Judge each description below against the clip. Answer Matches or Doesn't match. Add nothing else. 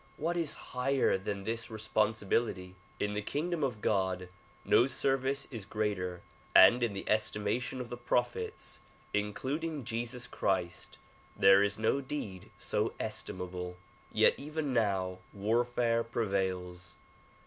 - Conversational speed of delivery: Doesn't match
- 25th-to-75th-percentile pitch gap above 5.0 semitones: Doesn't match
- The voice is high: Doesn't match